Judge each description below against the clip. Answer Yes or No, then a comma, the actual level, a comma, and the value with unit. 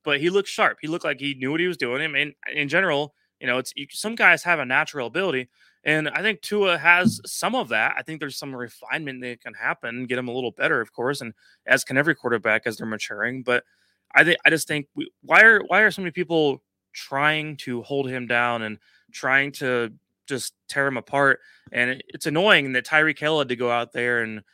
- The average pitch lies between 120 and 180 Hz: Yes, medium, 140 Hz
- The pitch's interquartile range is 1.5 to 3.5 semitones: No, average, 4.0 semitones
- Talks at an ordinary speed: No, fast, 230 wpm